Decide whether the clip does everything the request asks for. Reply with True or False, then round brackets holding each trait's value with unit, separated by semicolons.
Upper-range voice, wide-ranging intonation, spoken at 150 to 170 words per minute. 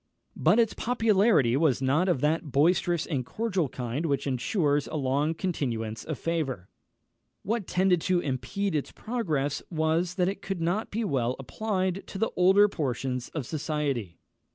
False (160 Hz; 5.9 semitones; 160 wpm)